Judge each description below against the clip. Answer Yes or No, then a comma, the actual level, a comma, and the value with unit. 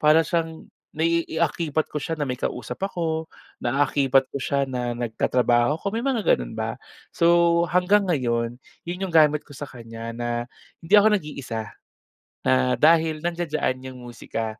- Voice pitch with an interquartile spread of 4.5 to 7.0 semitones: Yes, wide, 5.4 semitones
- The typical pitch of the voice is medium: Yes, medium, 150 Hz